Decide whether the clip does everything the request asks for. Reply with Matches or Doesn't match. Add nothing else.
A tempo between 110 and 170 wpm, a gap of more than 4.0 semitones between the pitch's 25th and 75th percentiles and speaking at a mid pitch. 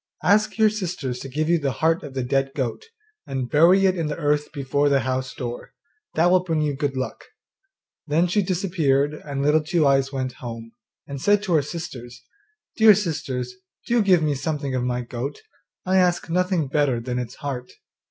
Doesn't match